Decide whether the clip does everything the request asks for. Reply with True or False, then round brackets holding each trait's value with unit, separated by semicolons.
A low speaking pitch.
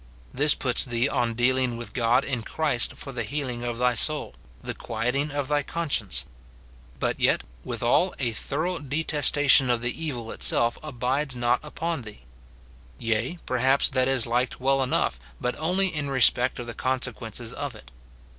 True (130 Hz)